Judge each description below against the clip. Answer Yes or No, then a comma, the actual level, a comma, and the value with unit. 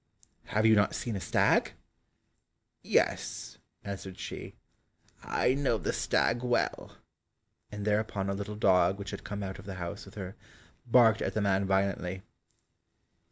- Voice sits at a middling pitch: No, low, 100 Hz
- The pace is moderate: Yes, average, 150 wpm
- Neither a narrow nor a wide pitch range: No, narrow, 2.1 semitones